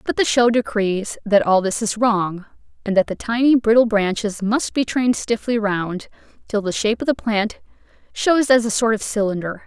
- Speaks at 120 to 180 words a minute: No, average, 200 wpm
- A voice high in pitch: Yes, high, 220 Hz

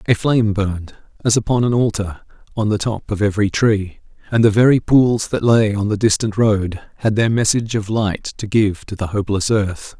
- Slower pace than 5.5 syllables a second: Yes, 5.2 syllables/s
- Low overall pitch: Yes, low, 105 Hz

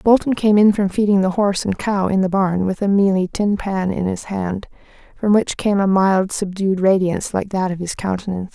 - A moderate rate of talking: No, fast, 225 wpm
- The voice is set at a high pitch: Yes, high, 195 Hz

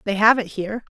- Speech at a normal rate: No, fast, 250 wpm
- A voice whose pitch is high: Yes, high, 210 Hz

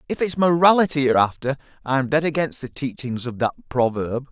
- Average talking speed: Yes, average, 195 wpm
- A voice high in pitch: No, low, 135 Hz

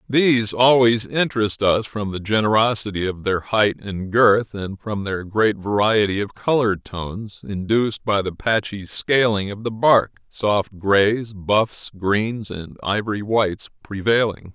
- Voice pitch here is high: No, low, 105 Hz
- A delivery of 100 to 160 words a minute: Yes, average, 145 wpm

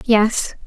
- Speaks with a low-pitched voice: No, high, 220 Hz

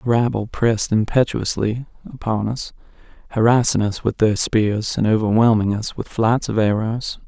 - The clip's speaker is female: No, male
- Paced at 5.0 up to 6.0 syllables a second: No, 4.8 syllables/s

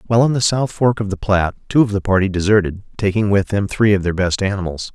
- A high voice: No, low, 100 Hz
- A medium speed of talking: No, fast, 255 wpm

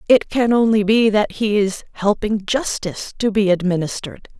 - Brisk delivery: No, average, 165 wpm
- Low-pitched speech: No, high, 210 Hz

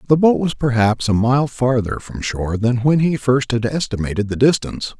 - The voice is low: Yes, low, 125 Hz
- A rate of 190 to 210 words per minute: Yes, fast, 205 wpm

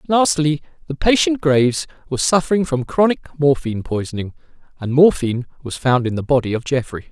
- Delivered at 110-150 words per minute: No, average, 160 wpm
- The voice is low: No, medium, 145 Hz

